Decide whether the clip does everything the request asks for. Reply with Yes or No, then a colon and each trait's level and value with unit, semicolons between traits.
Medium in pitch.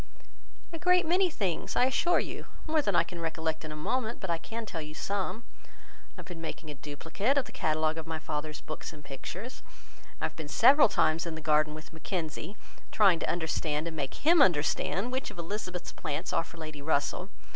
Yes: medium, 165 Hz